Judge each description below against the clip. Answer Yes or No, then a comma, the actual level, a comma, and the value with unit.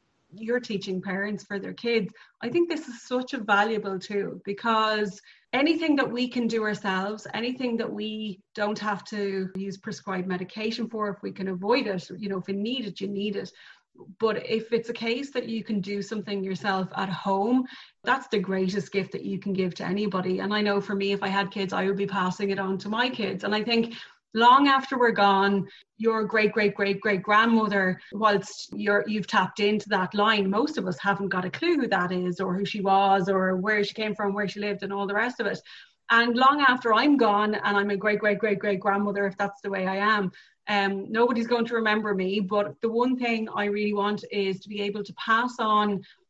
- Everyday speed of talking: No, fast, 225 wpm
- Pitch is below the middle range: No, high, 205 Hz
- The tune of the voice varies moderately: No, narrow, 2.2 semitones